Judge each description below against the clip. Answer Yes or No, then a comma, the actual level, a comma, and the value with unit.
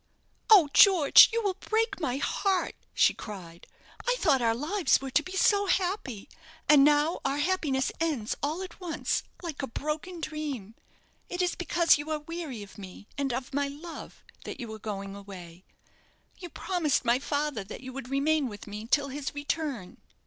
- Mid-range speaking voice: No, very high, 290 Hz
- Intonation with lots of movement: Yes, wide, 6.0 semitones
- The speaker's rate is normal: Yes, average, 180 wpm